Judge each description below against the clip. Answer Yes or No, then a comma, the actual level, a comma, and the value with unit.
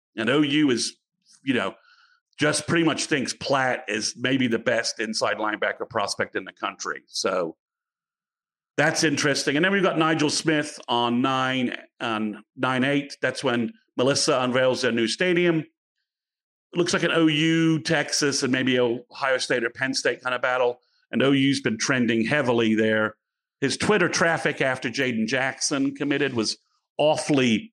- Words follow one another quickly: No, average, 160 wpm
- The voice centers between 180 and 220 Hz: No, medium, 140 Hz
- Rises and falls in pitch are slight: No, average, 4.1 semitones